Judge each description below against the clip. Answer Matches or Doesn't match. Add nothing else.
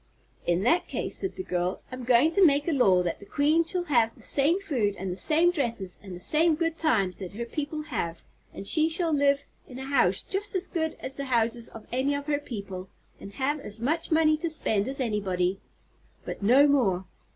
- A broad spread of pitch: Matches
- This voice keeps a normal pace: Doesn't match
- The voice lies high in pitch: Matches